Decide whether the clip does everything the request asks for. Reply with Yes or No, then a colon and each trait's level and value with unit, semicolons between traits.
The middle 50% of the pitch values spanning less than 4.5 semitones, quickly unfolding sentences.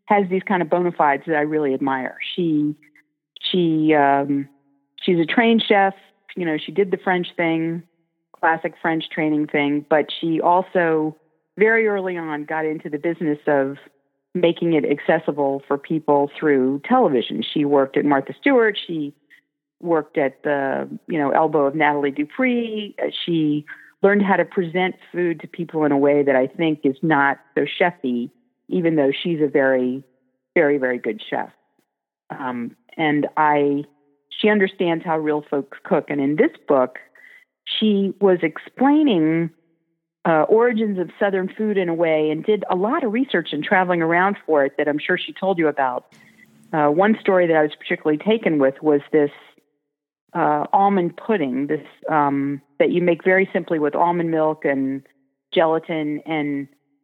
No: average, 3.9 semitones; average, 165 wpm